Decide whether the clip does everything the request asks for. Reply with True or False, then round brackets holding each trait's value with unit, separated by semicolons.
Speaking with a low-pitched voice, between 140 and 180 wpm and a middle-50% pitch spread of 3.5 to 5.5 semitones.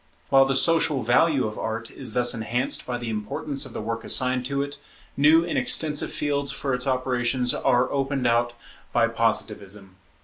False (130 Hz; 175 wpm; 3.0 semitones)